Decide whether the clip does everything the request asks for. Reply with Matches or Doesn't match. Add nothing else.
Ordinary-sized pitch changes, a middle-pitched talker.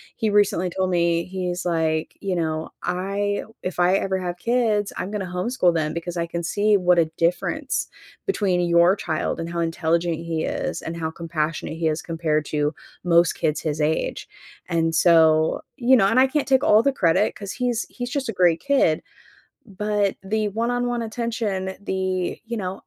Matches